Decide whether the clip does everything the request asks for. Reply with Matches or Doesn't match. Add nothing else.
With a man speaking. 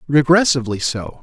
Matches